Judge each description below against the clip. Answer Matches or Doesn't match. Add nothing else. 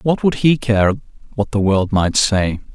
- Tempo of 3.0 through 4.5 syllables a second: Matches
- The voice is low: Matches